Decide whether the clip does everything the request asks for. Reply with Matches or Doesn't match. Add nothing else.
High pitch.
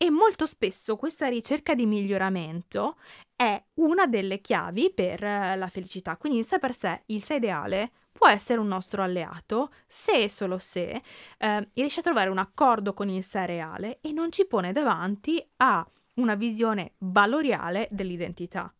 Matches